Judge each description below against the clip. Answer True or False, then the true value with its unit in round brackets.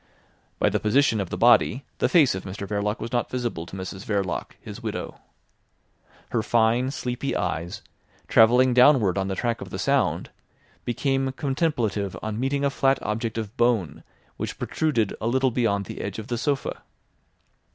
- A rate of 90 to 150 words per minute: False (170 wpm)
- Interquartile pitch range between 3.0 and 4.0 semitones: False (4.5 semitones)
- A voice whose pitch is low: True (115 Hz)